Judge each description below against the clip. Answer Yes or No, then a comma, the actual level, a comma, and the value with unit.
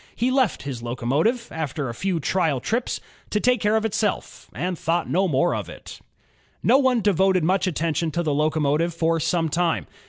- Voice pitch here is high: No, medium, 170 Hz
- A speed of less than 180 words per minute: No, average, 185 wpm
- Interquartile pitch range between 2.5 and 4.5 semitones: No, average, 5.0 semitones